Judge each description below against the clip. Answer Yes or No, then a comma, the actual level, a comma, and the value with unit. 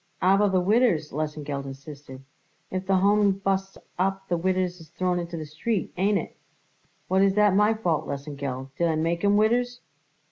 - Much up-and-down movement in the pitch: No, average, 4.2 semitones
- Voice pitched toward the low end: No, medium, 185 Hz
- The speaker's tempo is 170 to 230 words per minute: Yes, average, 175 wpm